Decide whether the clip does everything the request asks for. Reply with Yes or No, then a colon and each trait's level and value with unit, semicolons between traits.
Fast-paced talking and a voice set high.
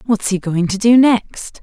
Yes: fast, 220 wpm; high, 215 Hz